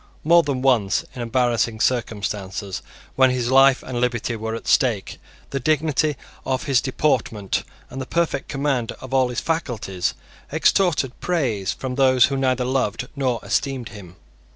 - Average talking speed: Yes, average, 155 wpm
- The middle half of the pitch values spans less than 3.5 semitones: Yes, average, 3.1 semitones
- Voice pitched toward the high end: No, low, 130 Hz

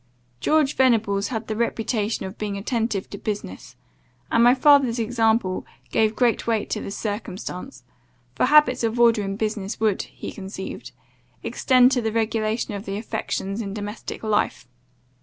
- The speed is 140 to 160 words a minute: Yes, average, 155 wpm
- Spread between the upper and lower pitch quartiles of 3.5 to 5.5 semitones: No, narrow, 2.5 semitones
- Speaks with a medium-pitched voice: No, high, 220 Hz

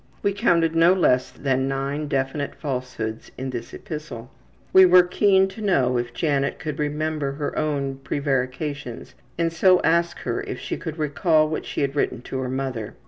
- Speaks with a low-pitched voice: No, medium, 145 Hz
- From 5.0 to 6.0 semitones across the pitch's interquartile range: No, average, 3.8 semitones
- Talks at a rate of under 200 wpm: Yes, average, 175 wpm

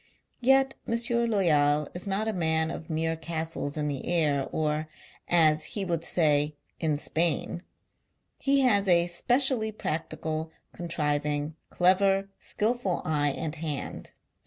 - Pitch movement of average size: Yes, average, 4.2 semitones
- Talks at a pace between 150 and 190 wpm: No, slow, 135 wpm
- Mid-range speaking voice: Yes, medium, 165 Hz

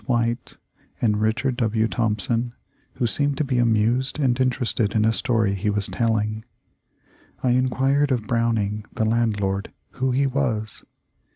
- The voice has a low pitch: Yes, low, 115 Hz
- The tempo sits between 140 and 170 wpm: Yes, average, 145 wpm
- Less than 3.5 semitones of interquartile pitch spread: Yes, average, 2.9 semitones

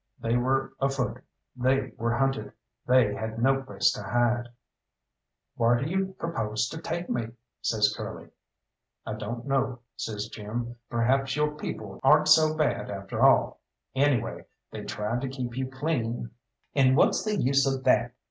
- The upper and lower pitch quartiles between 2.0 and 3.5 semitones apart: Yes, average, 2.7 semitones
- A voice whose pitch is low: Yes, low, 130 Hz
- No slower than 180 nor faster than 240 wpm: No, average, 155 wpm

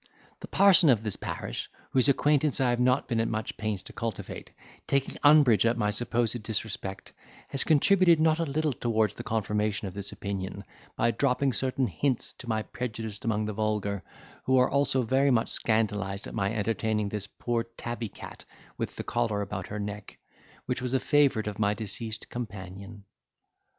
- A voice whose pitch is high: No, low, 115 Hz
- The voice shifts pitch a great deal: No, average, 3.8 semitones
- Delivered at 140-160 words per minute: No, average, 175 wpm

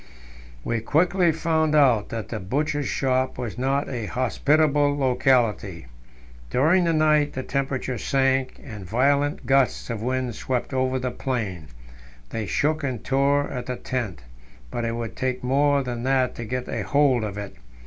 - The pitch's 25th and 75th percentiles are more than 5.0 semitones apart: No, average, 3.2 semitones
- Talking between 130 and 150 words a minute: No, average, 160 wpm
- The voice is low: Yes, low, 130 Hz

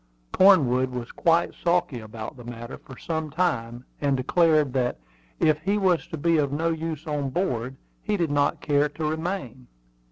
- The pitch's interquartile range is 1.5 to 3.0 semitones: No, average, 4.6 semitones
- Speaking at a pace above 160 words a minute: Yes, average, 170 wpm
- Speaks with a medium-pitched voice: Yes, medium, 150 Hz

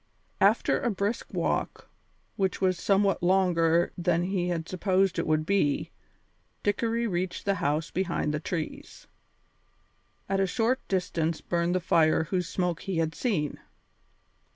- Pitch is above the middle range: No, medium, 180 Hz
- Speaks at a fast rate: No, average, 140 wpm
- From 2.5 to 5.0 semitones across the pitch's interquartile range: Yes, average, 2.8 semitones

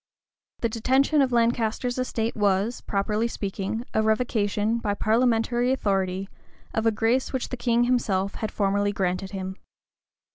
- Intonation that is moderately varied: Yes, average, 3.1 semitones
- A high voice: Yes, high, 220 Hz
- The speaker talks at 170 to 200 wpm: No, average, 140 wpm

